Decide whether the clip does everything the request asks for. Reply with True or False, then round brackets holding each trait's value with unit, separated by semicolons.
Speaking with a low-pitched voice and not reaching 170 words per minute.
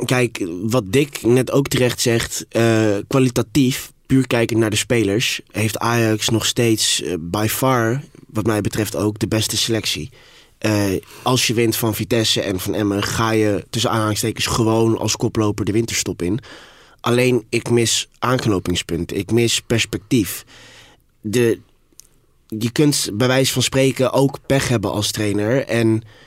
True (115 Hz; 155 wpm)